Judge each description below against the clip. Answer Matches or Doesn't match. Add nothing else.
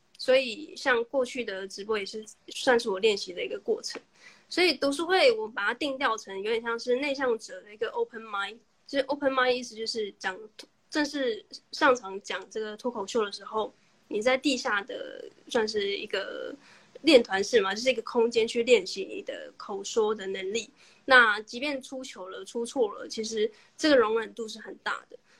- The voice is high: Matches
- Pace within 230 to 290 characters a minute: Doesn't match